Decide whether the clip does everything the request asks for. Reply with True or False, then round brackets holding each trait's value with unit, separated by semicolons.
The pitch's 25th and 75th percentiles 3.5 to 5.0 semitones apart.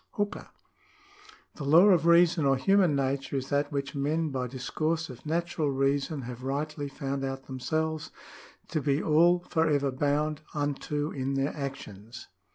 False (2.9 semitones)